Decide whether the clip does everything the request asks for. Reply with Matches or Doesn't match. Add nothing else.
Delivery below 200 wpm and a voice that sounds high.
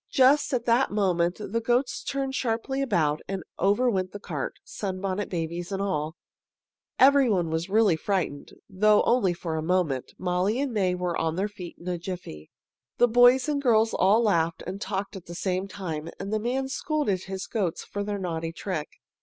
Matches